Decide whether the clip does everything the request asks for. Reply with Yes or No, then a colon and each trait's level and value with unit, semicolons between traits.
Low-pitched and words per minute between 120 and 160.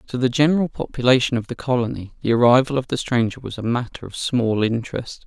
No: low, 125 Hz; fast, 205 wpm